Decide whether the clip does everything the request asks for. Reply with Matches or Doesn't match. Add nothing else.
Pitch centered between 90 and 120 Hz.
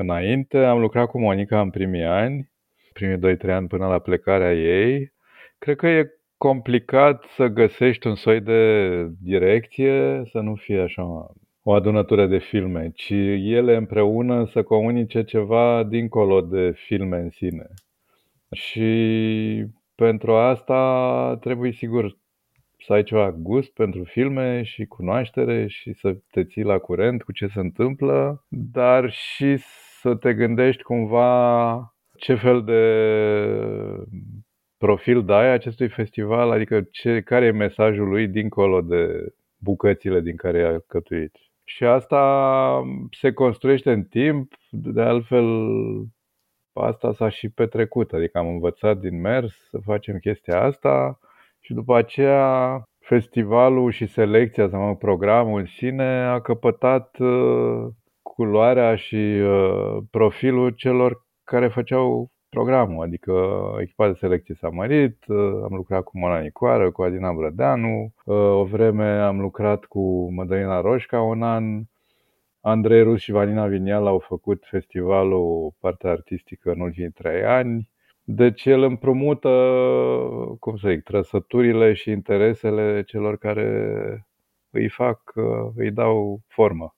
Matches